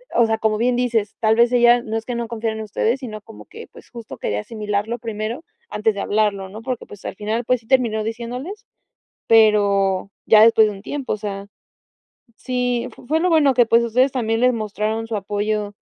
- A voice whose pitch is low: No, high, 225 Hz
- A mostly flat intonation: Yes, narrow, 2.3 semitones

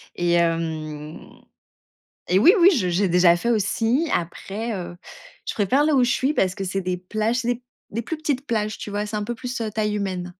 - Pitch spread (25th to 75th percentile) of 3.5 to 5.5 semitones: Yes, average, 5.1 semitones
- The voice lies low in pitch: No, high, 210 Hz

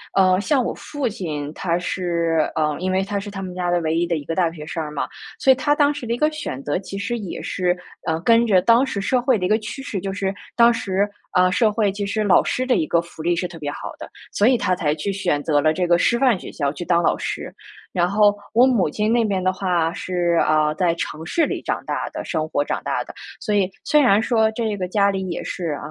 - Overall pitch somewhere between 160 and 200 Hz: Yes, high, 190 Hz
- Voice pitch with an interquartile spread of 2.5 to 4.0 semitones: No, average, 4.6 semitones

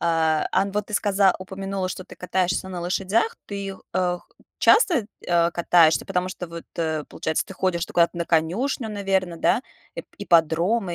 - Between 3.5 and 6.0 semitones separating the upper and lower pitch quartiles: No, narrow, 2.5 semitones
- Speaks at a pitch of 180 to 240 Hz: Yes, medium, 185 Hz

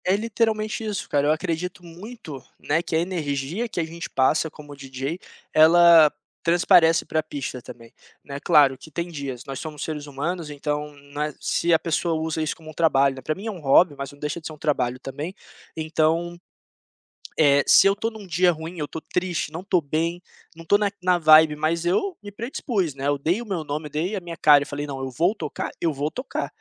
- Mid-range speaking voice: Yes, medium, 160 Hz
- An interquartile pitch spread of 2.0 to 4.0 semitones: Yes, average, 3.4 semitones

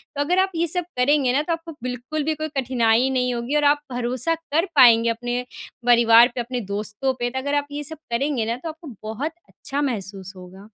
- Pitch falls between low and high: No, very high, 255 Hz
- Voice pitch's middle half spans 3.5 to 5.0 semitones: Yes, average, 4.0 semitones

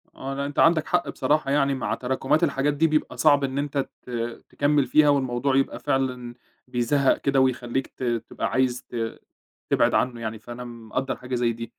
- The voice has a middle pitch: No, low, 130 Hz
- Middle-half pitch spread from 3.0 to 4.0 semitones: No, narrow, 2.6 semitones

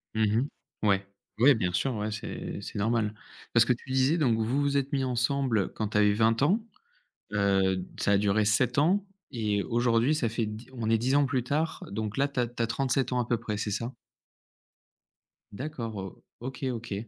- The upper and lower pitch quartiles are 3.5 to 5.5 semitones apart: Yes, average, 3.8 semitones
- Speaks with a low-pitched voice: Yes, low, 115 Hz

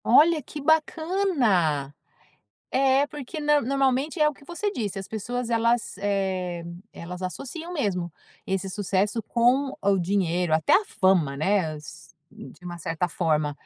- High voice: Yes, high, 205 Hz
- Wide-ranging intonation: Yes, wide, 7.7 semitones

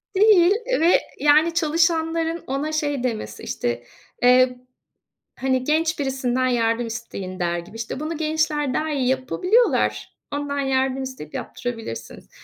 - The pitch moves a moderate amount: Yes, average, 4.5 semitones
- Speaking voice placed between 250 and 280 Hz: Yes, very high, 270 Hz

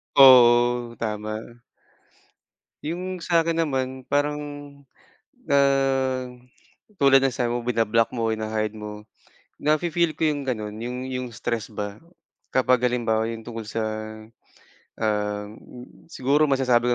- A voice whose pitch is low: Yes, low, 120 Hz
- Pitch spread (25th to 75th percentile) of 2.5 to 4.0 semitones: Yes, average, 3.7 semitones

